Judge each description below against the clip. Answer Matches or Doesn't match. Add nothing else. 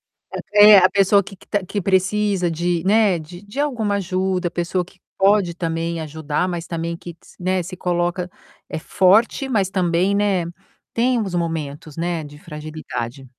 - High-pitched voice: Doesn't match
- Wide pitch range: Doesn't match